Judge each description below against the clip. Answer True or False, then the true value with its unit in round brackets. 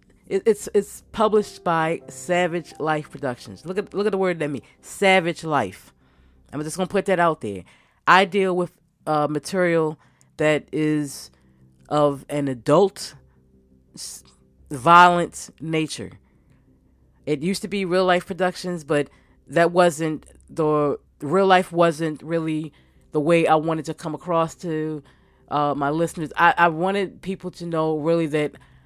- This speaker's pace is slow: False (145 wpm)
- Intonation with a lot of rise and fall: False (3.9 semitones)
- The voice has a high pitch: False (160 Hz)